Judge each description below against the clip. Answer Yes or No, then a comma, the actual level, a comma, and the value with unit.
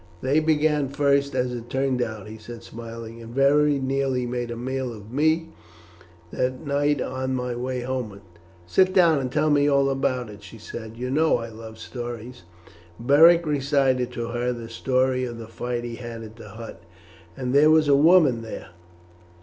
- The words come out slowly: No, average, 175 wpm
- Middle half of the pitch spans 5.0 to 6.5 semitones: No, average, 3.2 semitones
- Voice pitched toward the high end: No, low, 125 Hz